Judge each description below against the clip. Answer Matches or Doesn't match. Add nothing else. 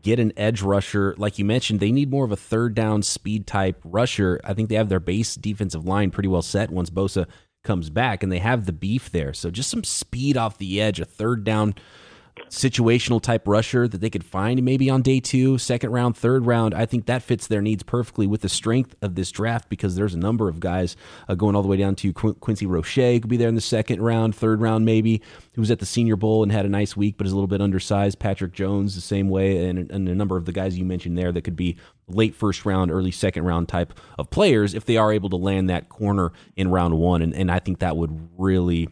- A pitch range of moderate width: Matches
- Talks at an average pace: Doesn't match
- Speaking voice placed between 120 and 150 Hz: Doesn't match